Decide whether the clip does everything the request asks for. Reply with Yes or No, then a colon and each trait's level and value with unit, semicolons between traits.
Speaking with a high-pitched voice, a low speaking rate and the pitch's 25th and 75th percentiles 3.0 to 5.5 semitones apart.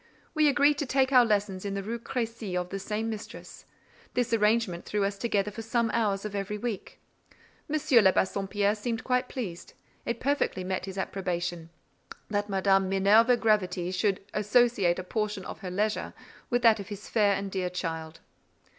No: high, 205 Hz; average, 175 wpm; average, 3.3 semitones